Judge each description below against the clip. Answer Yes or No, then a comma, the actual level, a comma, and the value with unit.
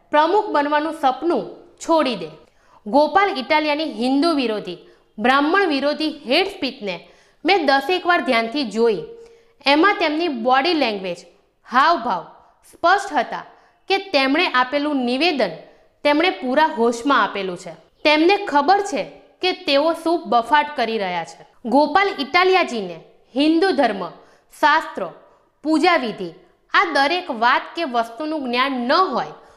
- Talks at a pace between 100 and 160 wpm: Yes, average, 120 wpm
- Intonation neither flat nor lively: No, wide, 6.1 semitones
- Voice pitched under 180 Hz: No, very high, 295 Hz